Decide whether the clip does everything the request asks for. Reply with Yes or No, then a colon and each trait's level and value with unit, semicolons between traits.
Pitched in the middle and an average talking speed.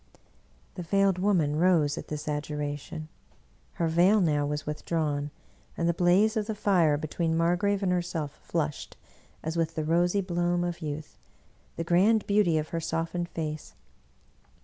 Yes: medium, 165 Hz; average, 160 wpm